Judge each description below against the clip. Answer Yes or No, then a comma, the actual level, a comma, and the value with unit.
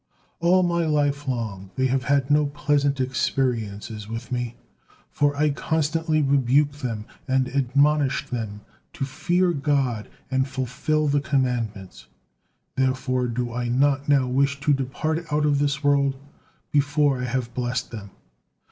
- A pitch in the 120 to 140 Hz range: Yes, low, 135 Hz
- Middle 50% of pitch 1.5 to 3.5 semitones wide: Yes, average, 2.7 semitones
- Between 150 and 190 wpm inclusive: No, average, 140 wpm